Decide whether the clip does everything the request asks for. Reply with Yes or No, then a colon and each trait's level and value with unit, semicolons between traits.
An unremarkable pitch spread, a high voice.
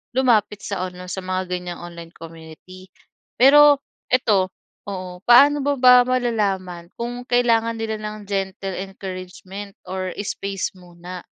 Yes: average, 4.6 semitones; high, 195 Hz